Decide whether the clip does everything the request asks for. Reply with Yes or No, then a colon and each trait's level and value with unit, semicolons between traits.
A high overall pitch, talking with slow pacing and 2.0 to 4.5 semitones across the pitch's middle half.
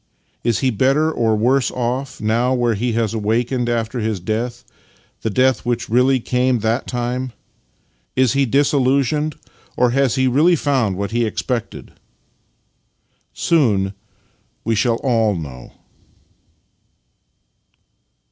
No: low, 120 Hz; slow, 125 wpm; average, 2.7 semitones